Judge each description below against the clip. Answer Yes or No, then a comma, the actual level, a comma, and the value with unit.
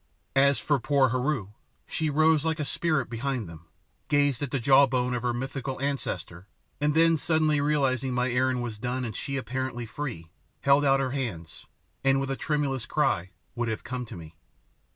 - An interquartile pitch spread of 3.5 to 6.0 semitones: No, average, 2.9 semitones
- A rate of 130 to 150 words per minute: No, average, 185 wpm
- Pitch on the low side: Yes, low, 130 Hz